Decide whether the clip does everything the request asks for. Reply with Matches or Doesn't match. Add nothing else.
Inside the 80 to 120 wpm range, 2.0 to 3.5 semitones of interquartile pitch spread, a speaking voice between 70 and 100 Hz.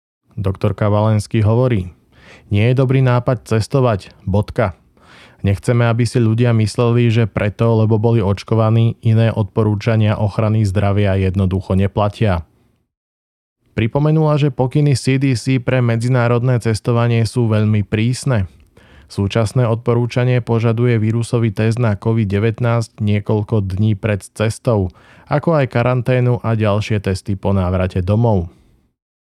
Doesn't match